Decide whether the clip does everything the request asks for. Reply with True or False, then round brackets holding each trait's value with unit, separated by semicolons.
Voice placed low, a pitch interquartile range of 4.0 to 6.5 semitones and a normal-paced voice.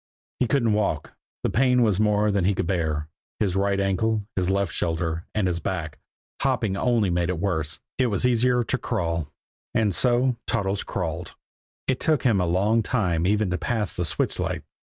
True (100 Hz; 4.4 semitones; 185 wpm)